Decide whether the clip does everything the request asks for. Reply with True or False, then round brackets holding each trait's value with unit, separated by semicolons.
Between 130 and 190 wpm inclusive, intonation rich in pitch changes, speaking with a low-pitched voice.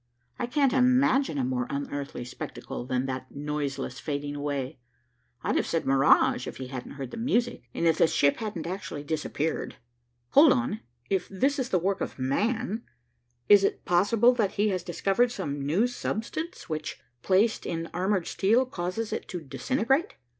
False (170 wpm; 8.6 semitones; 185 Hz)